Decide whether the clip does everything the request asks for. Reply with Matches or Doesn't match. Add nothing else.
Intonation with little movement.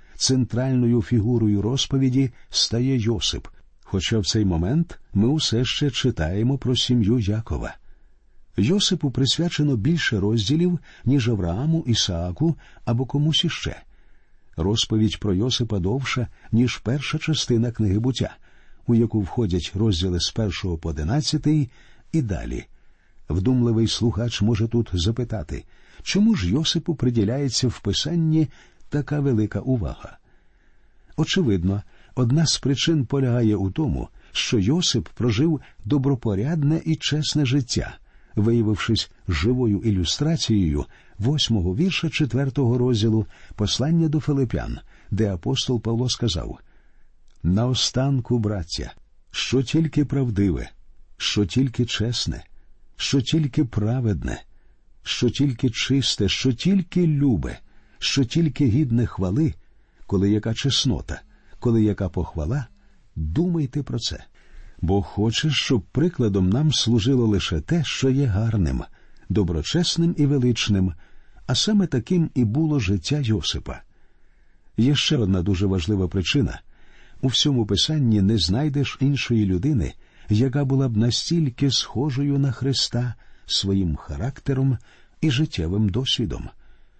Doesn't match